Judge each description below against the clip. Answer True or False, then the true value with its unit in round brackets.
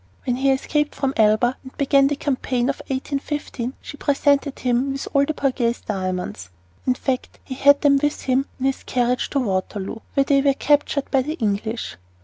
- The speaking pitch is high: True (265 Hz)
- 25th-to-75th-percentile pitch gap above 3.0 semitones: False (2.6 semitones)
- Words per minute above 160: True (185 wpm)